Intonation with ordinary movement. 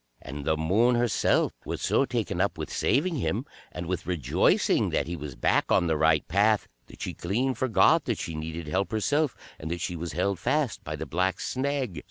No: wide, 6.9 semitones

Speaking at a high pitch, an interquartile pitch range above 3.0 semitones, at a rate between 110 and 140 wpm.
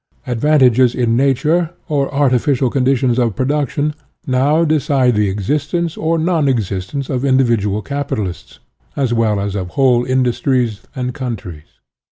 No: low, 130 Hz; average, 3.7 semitones; slow, 135 wpm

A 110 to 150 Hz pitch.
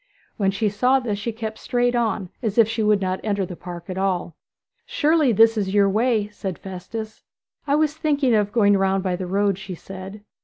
No: high, 205 Hz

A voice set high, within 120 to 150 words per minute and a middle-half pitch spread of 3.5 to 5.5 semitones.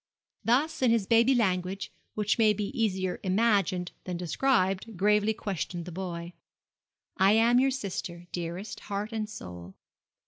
Yes: high, 200 Hz; average, 140 wpm; average, 3.8 semitones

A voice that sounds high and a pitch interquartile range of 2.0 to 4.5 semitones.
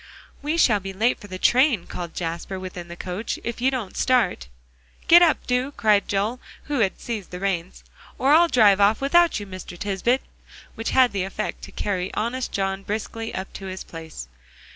No: high, 205 Hz; average, 5.0 semitones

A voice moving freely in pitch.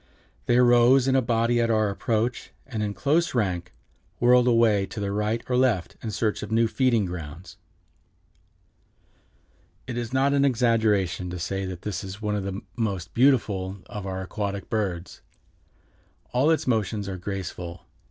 No: average, 3.8 semitones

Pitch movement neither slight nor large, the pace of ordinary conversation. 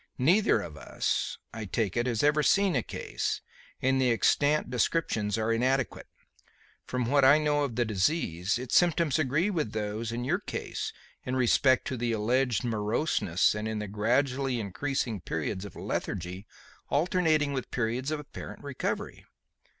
Yes: average, 4.9 semitones; average, 160 wpm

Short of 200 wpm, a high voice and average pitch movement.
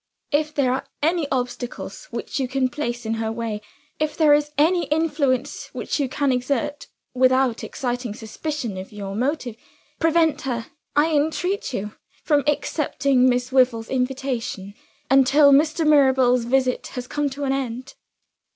Yes: average, 150 wpm; very high, 265 Hz; average, 3.2 semitones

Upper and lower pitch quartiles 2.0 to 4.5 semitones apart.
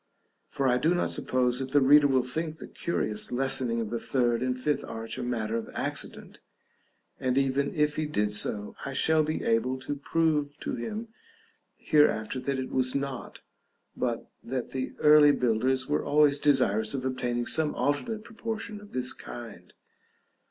Yes: average, 3.4 semitones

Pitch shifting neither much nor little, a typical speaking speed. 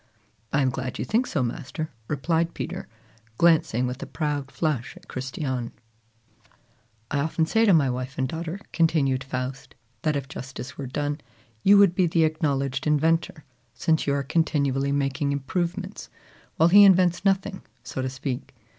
Yes: average, 3.9 semitones; average, 160 wpm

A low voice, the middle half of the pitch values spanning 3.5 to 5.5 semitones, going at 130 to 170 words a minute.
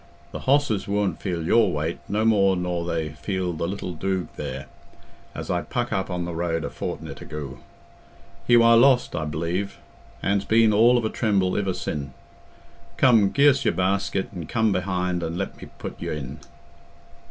No: very low, 95 Hz; average, 4.2 semitones; average, 180 wpm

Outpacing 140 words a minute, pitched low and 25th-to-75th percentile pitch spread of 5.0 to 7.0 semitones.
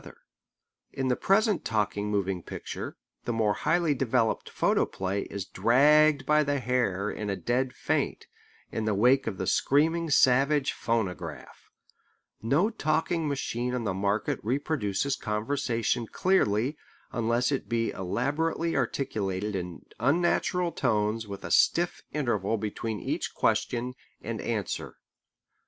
No: slow, 135 wpm; low, 120 Hz; wide, 5.4 semitones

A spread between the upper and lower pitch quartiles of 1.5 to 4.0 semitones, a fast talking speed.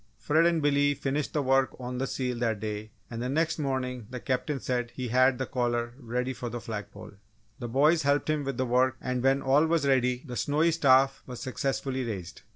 Yes: narrow, 2.5 semitones; fast, 215 wpm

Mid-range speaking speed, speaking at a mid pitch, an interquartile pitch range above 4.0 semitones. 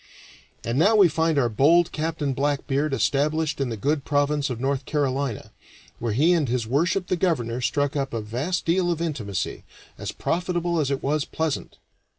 No: average, 175 wpm; medium, 145 Hz; average, 3.6 semitones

